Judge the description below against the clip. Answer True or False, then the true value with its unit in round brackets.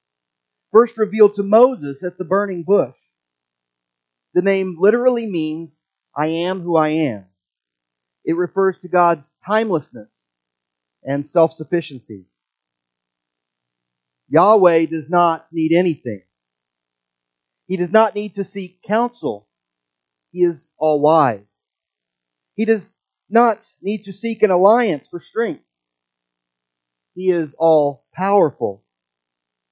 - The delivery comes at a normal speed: False (105 wpm)